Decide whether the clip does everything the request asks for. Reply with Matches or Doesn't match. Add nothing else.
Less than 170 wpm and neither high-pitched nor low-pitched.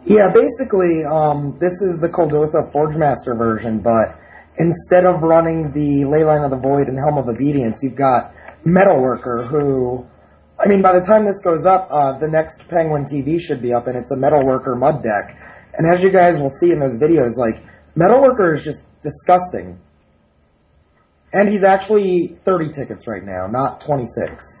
Doesn't match